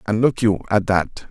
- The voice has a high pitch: No, low, 105 Hz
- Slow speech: No, fast, 230 wpm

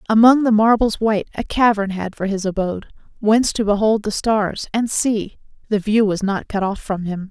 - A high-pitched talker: Yes, high, 210 Hz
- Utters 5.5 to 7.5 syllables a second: No, 5.2 syllables/s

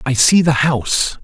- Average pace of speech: Yes, average, 195 wpm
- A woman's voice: No, male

